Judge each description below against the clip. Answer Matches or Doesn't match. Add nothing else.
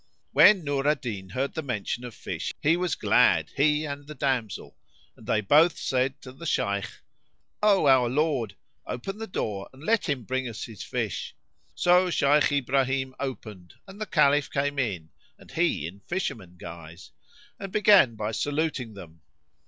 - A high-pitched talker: Doesn't match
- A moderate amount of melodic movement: Doesn't match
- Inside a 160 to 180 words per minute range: Matches